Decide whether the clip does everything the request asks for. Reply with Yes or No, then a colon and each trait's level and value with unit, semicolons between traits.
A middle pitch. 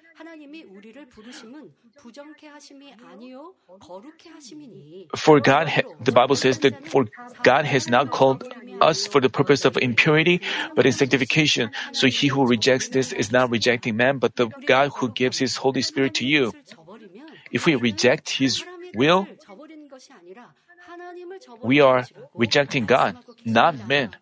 Yes: medium, 145 Hz